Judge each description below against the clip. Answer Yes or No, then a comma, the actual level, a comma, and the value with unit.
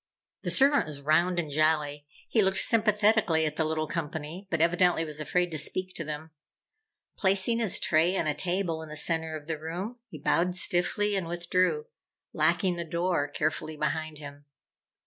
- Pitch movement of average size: Yes, average, 3.1 semitones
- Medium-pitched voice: Yes, medium, 165 Hz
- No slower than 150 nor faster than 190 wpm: Yes, average, 175 wpm